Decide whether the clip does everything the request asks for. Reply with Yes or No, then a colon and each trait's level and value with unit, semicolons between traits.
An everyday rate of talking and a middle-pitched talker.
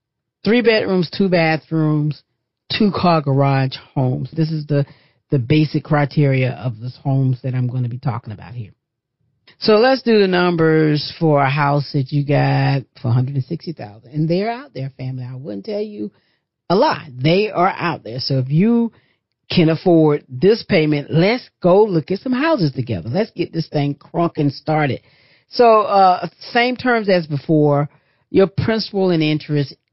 Yes: average, 165 wpm; medium, 150 Hz